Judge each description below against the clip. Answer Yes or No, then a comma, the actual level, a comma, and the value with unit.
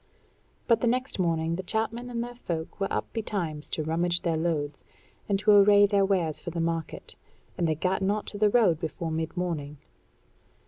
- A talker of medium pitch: Yes, medium, 180 Hz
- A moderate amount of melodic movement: Yes, average, 4.3 semitones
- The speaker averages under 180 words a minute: No, average, 190 wpm